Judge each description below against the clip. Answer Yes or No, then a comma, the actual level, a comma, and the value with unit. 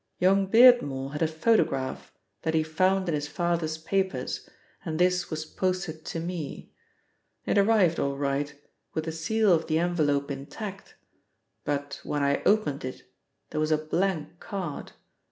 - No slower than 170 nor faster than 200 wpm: No, average, 155 wpm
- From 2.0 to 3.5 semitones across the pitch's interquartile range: No, average, 4.1 semitones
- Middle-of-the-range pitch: Yes, medium, 160 Hz